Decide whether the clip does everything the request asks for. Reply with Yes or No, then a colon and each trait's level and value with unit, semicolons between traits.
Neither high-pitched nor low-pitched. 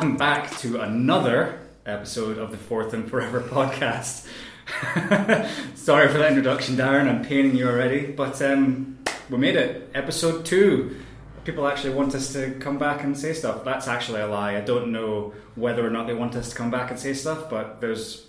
No: low, 130 Hz